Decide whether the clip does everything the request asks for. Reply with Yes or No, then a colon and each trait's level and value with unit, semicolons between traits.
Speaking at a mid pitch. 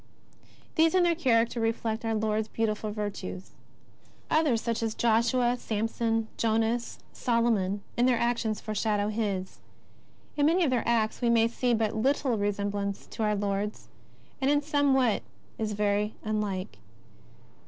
No: high, 225 Hz